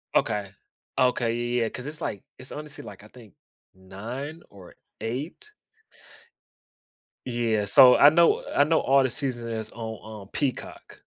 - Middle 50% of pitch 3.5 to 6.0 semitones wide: Yes, average, 4.2 semitones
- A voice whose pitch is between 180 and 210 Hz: No, low, 120 Hz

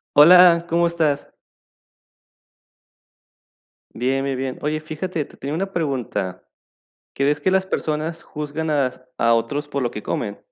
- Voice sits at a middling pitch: Yes, medium, 150 Hz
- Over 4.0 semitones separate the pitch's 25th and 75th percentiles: No, average, 3.7 semitones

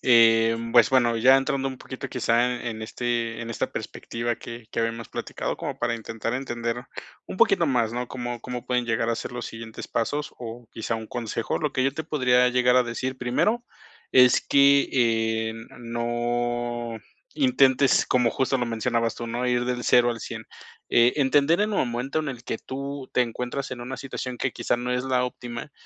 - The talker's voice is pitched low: Yes, low, 120 Hz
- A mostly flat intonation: Yes, narrow, 2.0 semitones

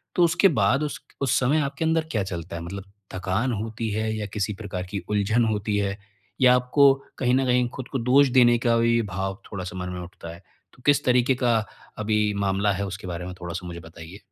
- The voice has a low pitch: Yes, low, 105 Hz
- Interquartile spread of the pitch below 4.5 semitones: No, average, 5.0 semitones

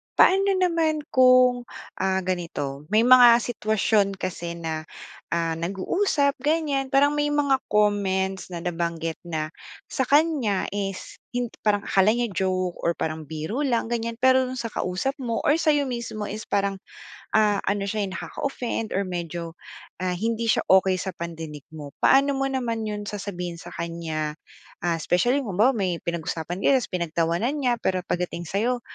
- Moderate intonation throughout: No, wide, 6.5 semitones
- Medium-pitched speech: No, high, 205 Hz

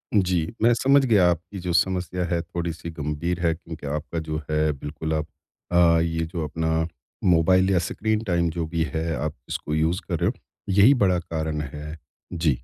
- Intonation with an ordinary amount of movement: No, narrow, 2.3 semitones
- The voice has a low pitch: Yes, very low, 85 Hz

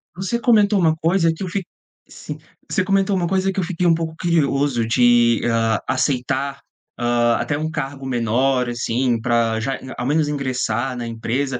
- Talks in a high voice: No, low, 135 Hz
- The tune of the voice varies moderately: No, wide, 5.8 semitones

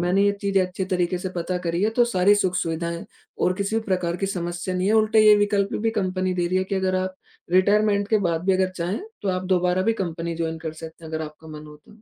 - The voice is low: No, medium, 185 Hz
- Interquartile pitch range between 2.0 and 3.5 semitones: Yes, average, 2.9 semitones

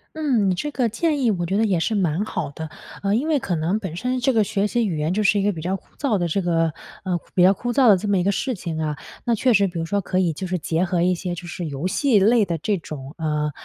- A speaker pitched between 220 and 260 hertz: No, high, 190 Hz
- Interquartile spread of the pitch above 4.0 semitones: Yes, average, 4.6 semitones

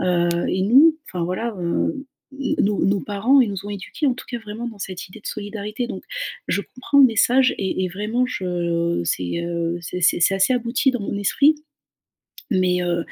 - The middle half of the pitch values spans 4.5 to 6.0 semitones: Yes, average, 5.0 semitones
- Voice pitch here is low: No, high, 200 Hz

